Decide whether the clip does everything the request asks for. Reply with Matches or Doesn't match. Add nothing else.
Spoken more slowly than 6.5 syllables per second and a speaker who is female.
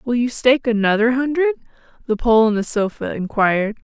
Matches